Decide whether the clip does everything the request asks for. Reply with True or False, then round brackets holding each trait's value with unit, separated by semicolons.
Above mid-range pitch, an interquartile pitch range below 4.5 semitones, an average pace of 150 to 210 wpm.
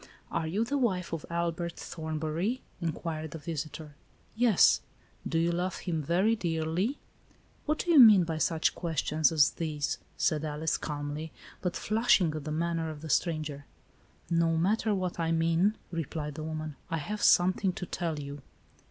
False (165 Hz; 2.7 semitones; 185 wpm)